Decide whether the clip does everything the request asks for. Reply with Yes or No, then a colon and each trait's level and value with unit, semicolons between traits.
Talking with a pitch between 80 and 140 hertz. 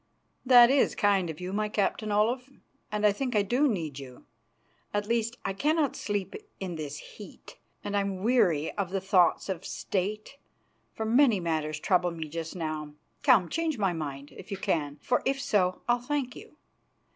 No: high, 200 Hz